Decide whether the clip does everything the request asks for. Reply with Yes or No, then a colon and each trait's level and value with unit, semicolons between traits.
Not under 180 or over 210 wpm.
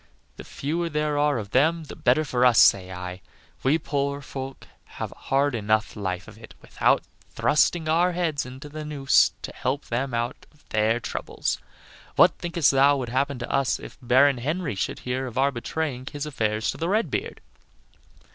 Yes: average, 185 wpm